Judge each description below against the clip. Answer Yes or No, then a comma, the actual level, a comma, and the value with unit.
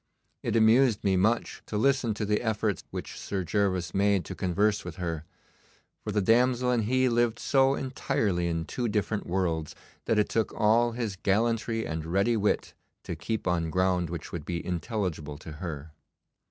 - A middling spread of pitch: Yes, average, 4.6 semitones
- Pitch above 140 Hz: No, low, 105 Hz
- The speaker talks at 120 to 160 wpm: No, average, 175 wpm